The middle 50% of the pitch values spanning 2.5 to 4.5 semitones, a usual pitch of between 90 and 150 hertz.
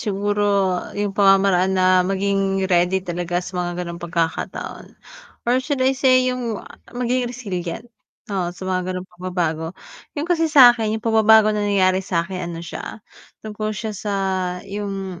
No: average, 3.4 semitones; high, 195 Hz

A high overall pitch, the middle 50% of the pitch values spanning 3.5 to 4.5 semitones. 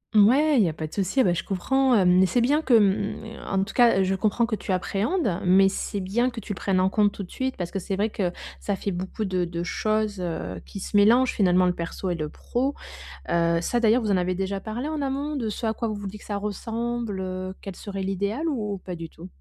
Yes: high, 200 Hz; average, 3.9 semitones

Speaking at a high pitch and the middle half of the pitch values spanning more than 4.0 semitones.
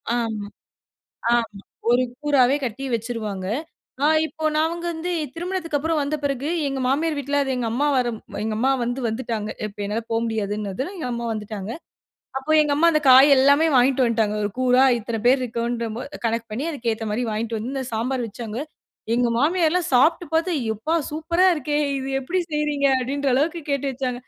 Yes: very high, 255 Hz; average, 4.6 semitones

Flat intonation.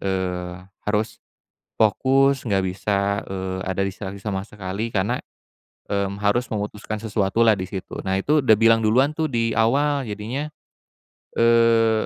No: average, 3.1 semitones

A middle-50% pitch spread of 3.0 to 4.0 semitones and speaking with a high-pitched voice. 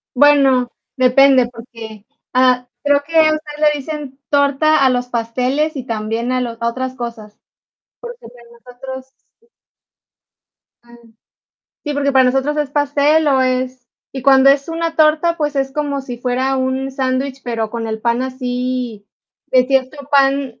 No: narrow, 2.5 semitones; very high, 260 Hz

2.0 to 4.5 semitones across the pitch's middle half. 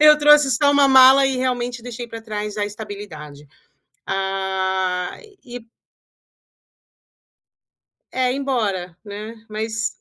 No: average, 4.9 semitones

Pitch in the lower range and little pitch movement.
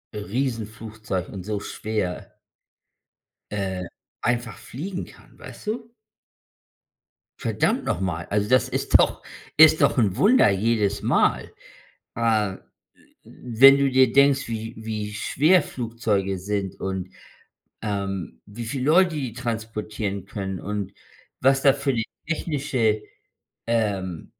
No: low, 110 Hz; average, 4.7 semitones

